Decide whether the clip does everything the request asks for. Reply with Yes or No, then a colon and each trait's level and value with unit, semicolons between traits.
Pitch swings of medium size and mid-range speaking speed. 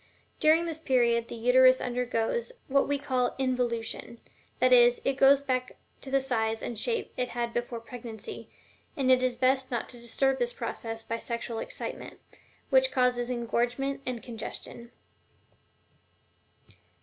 No: narrow, 2.2 semitones; average, 145 wpm